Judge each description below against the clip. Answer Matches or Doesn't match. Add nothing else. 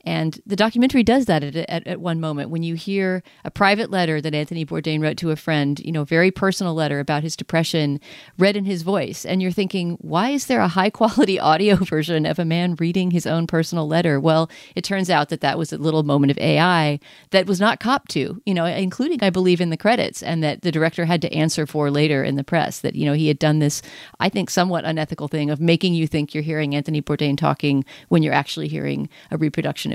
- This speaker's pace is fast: Matches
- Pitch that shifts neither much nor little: Matches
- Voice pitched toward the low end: Doesn't match